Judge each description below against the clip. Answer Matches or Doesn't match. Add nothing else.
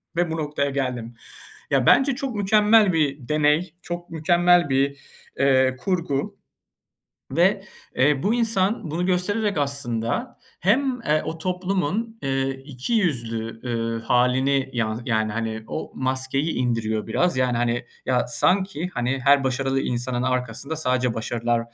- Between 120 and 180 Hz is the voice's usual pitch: Matches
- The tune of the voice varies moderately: Doesn't match